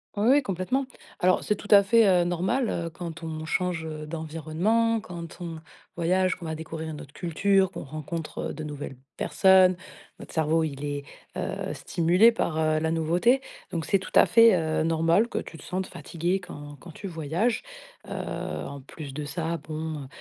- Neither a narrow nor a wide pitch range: Yes, average, 3.1 semitones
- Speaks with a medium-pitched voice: Yes, medium, 165 Hz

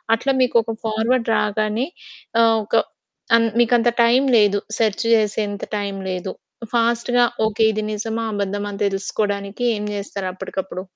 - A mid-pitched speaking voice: No, high, 215 Hz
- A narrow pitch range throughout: Yes, narrow, 2.2 semitones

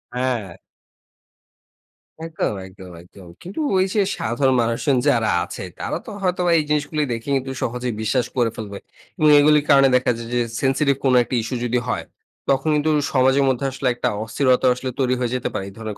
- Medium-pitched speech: No, low, 130 Hz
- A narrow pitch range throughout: No, average, 3.3 semitones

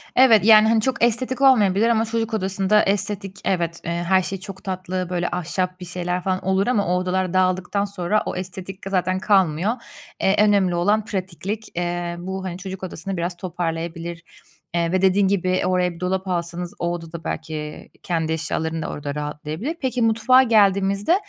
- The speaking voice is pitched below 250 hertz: Yes, medium, 185 Hz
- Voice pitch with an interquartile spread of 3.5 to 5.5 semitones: No, average, 2.7 semitones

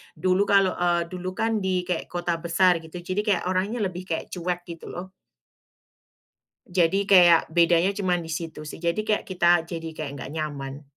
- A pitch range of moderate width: No, narrow, 2.0 semitones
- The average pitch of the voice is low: No, medium, 175 Hz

